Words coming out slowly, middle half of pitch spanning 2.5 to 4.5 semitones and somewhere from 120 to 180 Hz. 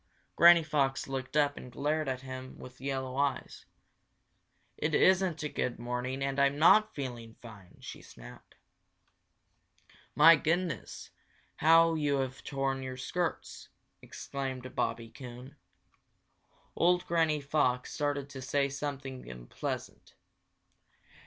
Yes: slow, 120 wpm; average, 2.9 semitones; medium, 140 Hz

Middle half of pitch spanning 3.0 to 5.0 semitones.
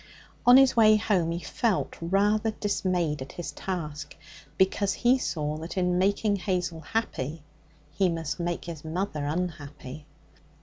Yes: average, 4.2 semitones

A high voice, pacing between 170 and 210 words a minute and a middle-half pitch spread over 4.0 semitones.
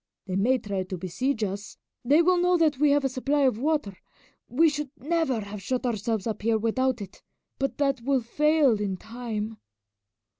Yes: very high, 250 Hz; average, 185 wpm; average, 5.3 semitones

